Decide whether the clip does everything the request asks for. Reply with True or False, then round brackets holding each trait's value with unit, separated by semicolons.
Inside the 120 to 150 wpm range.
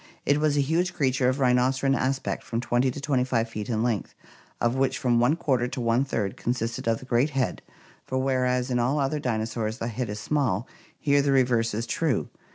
False (205 wpm)